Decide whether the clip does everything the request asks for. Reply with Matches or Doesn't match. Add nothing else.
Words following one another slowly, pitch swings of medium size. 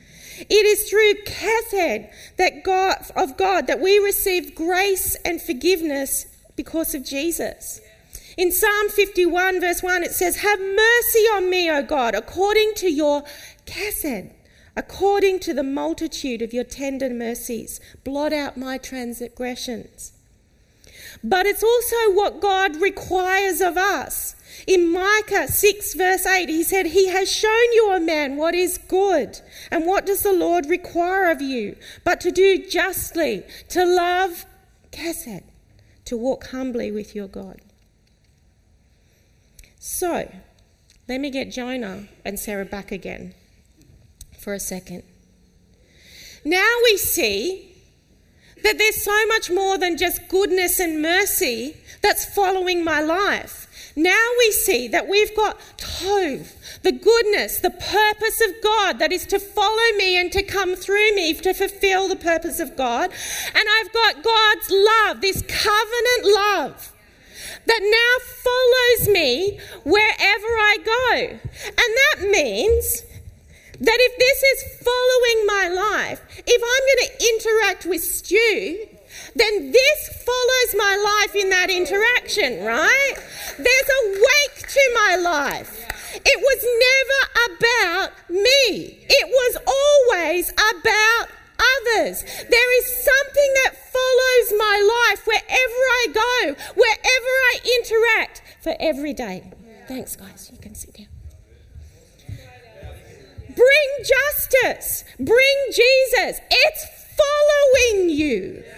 Doesn't match